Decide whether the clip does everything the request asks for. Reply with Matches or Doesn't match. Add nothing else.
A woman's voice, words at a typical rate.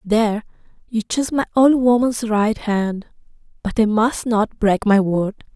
Matches